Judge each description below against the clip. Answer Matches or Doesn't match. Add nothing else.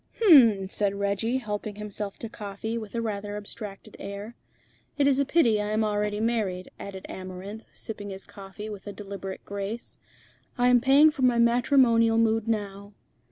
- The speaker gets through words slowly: Doesn't match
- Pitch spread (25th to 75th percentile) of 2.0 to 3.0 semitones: Matches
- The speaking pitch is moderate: Doesn't match